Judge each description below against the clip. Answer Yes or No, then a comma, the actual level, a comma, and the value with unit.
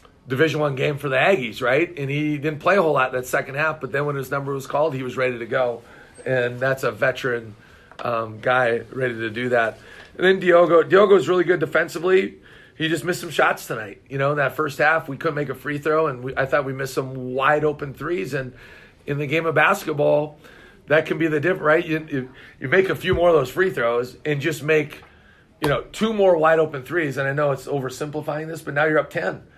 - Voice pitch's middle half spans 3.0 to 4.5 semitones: Yes, average, 3.5 semitones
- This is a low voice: No, medium, 145 Hz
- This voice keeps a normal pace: No, fast, 240 wpm